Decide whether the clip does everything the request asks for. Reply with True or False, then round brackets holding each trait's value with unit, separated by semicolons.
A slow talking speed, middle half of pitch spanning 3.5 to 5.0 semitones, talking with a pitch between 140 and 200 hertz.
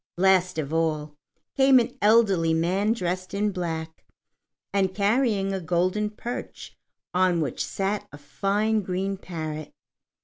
True (130 wpm; 4.0 semitones; 185 Hz)